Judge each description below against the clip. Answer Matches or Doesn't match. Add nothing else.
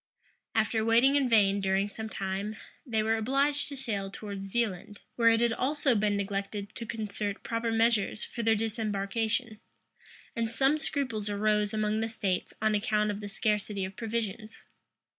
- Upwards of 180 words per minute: Doesn't match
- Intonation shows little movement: Matches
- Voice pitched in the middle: Doesn't match